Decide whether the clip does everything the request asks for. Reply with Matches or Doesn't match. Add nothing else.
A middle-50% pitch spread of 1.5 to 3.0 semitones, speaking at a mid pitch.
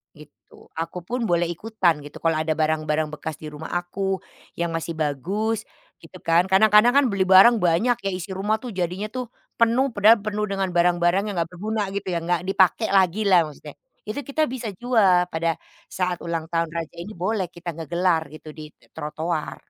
Doesn't match